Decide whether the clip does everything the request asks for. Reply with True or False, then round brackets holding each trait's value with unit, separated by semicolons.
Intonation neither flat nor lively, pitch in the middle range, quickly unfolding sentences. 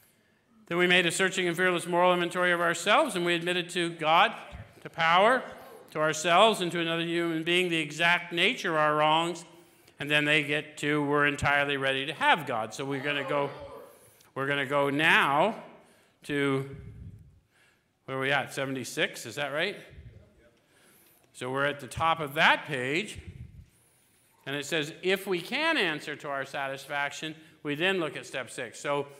False (3.6 semitones; 155 Hz; 175 wpm)